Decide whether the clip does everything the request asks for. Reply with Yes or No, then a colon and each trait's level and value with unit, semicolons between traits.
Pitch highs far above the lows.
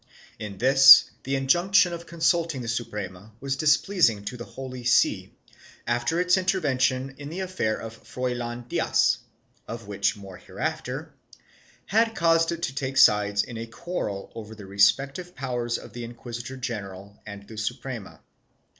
Yes: wide, 5.9 semitones